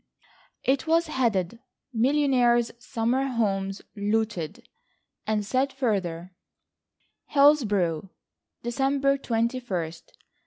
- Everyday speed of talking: No, slow, 75 wpm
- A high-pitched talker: Yes, high, 235 Hz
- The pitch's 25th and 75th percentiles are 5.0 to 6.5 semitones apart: Yes, average, 5.3 semitones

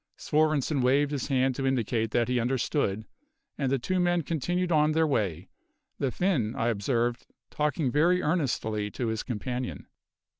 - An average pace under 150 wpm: No, average, 155 wpm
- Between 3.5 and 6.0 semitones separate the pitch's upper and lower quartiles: Yes, average, 4.5 semitones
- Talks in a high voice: No, low, 130 Hz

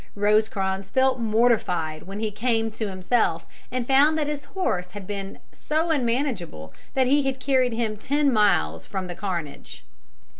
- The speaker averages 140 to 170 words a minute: Yes, average, 155 wpm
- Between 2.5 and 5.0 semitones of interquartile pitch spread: No, wide, 5.5 semitones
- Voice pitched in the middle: No, high, 220 Hz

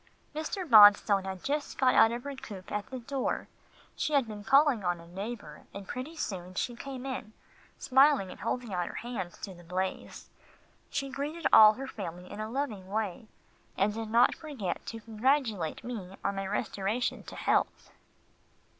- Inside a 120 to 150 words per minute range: No, average, 175 wpm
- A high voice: Yes, high, 220 Hz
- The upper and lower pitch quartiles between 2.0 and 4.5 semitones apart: No, wide, 5.4 semitones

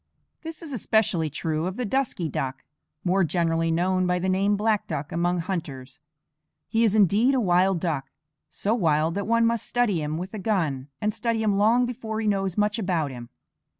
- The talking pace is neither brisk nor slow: Yes, average, 190 wpm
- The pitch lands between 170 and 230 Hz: Yes, high, 190 Hz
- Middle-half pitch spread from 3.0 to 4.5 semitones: No, average, 4.9 semitones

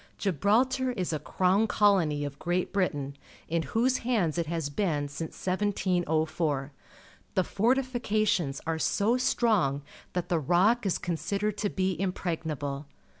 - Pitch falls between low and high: Yes, medium, 180 Hz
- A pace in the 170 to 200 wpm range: No, slow, 135 wpm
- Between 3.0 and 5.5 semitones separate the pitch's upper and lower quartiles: Yes, average, 5.0 semitones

